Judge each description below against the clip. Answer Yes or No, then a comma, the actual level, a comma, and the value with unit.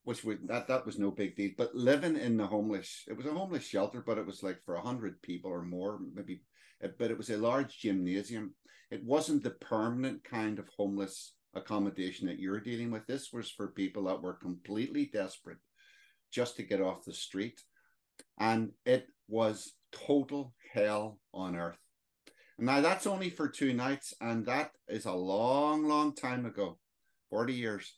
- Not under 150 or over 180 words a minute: Yes, average, 175 wpm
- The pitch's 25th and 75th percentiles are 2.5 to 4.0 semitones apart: No, average, 4.5 semitones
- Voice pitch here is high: No, low, 110 Hz